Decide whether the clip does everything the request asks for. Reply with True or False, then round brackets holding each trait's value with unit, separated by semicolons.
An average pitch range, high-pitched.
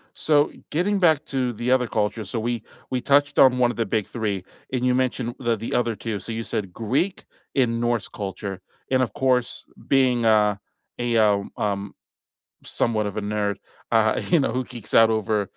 False (3.2 semitones; 115 Hz)